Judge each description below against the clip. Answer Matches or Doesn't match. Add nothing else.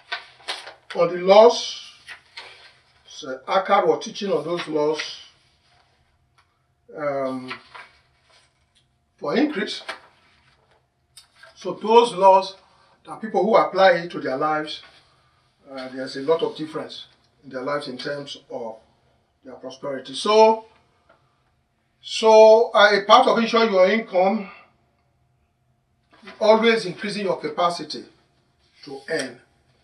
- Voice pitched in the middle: Matches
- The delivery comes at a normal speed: Doesn't match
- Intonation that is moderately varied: Doesn't match